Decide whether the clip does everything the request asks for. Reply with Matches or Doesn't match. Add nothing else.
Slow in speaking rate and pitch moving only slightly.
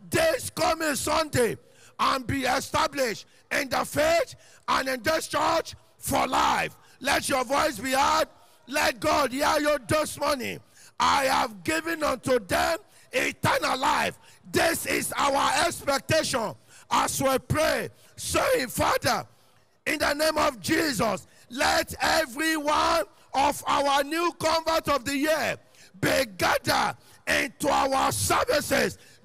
Matches